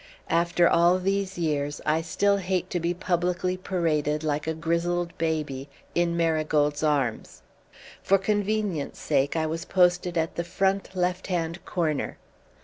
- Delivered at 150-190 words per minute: No, average, 140 wpm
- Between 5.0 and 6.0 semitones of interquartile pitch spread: No, average, 2.7 semitones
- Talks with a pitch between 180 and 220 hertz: No, medium, 170 Hz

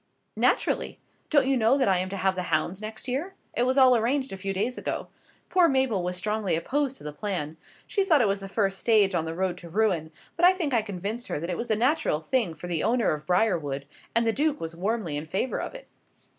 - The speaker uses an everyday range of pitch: No, wide, 6.3 semitones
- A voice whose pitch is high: Yes, high, 210 Hz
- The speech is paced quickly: Yes, fast, 245 wpm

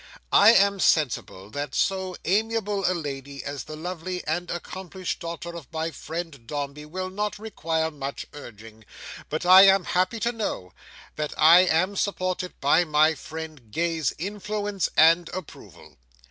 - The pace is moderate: Yes, average, 145 wpm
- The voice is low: No, medium, 170 Hz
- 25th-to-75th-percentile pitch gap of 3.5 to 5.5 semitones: Yes, average, 3.8 semitones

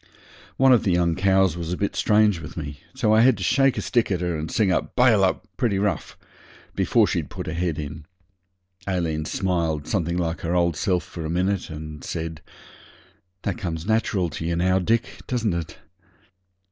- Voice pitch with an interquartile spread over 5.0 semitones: No, average, 4.1 semitones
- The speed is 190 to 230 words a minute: Yes, average, 195 wpm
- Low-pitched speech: Yes, very low, 90 Hz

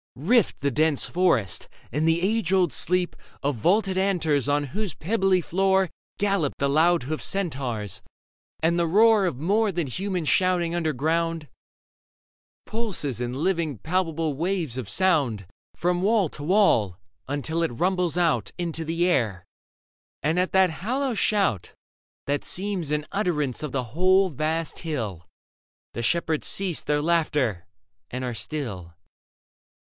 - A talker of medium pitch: Yes, medium, 165 Hz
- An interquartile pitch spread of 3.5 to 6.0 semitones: Yes, average, 4.8 semitones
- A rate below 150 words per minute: Yes, average, 140 wpm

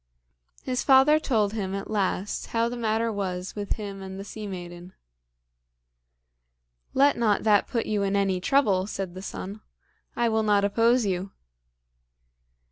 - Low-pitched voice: No, high, 205 Hz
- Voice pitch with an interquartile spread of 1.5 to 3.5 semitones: Yes, average, 3.0 semitones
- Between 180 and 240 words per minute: No, average, 150 wpm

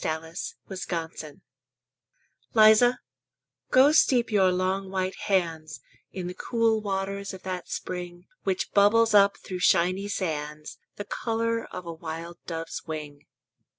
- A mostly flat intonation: No, average, 3.6 semitones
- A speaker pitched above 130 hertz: Yes, medium, 185 Hz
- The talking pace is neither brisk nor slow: No, slow, 125 wpm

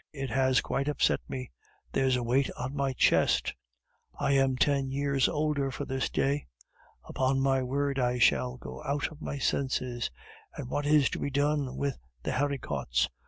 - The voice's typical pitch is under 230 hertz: Yes, low, 135 Hz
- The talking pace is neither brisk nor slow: Yes, average, 170 wpm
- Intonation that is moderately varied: No, narrow, 1.8 semitones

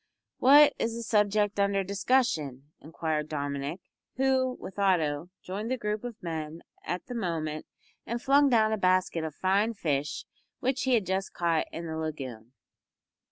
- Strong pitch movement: Yes, wide, 6.4 semitones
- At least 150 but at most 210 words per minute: Yes, average, 160 wpm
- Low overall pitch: No, high, 190 Hz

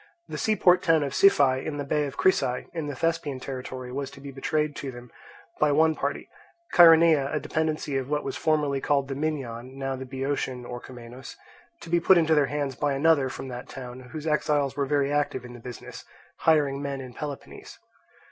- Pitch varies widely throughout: No, average, 2.7 semitones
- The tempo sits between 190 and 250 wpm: Yes, average, 195 wpm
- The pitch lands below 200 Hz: Yes, medium, 140 Hz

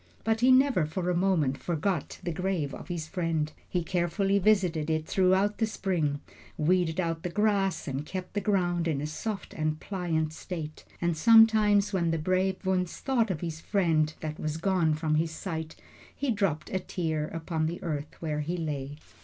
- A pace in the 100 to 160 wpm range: No, average, 185 wpm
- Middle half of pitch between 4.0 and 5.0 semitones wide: No, average, 3.6 semitones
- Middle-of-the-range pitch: Yes, medium, 175 Hz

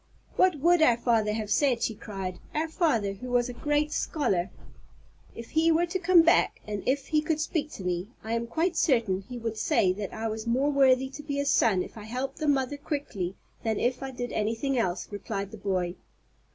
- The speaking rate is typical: No, fast, 215 wpm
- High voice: Yes, high, 245 Hz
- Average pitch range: No, wide, 5.7 semitones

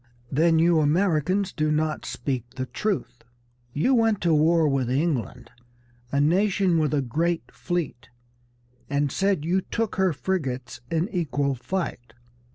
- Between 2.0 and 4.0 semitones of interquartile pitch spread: No, average, 4.8 semitones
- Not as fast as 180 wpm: Yes, average, 140 wpm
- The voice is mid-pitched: Yes, medium, 160 Hz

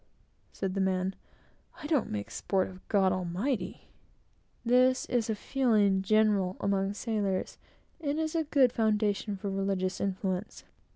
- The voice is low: No, high, 200 Hz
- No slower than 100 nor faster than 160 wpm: Yes, slow, 135 wpm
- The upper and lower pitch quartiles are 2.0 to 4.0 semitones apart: Yes, average, 3.7 semitones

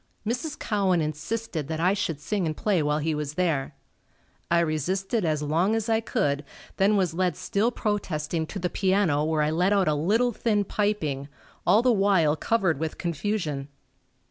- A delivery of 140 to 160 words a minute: No, average, 175 wpm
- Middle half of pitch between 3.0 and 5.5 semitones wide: Yes, average, 5.1 semitones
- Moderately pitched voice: Yes, medium, 180 Hz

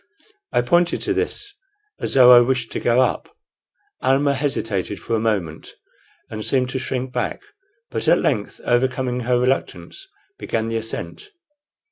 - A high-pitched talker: No, low, 125 Hz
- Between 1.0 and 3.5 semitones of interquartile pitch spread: Yes, narrow, 2.6 semitones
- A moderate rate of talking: Yes, average, 150 wpm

